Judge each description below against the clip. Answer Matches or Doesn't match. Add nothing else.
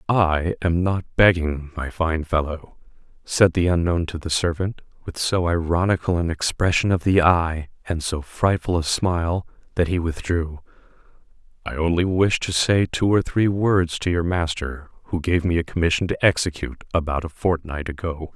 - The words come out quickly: Doesn't match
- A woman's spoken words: Doesn't match